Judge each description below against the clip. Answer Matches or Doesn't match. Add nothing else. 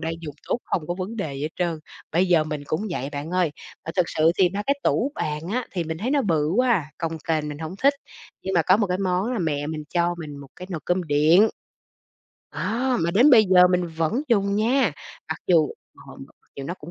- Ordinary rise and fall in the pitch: Matches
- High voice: Doesn't match